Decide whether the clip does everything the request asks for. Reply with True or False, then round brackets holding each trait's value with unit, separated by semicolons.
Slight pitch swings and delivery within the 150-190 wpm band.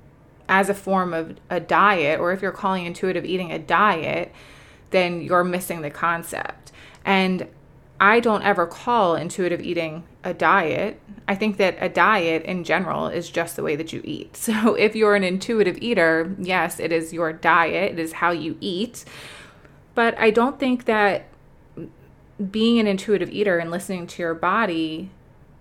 False (3.3 semitones; 170 wpm)